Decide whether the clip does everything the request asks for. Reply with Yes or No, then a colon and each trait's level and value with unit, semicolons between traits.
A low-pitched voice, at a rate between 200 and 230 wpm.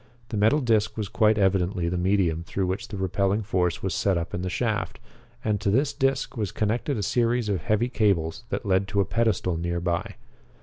Yes: low, 100 Hz; fast, 205 wpm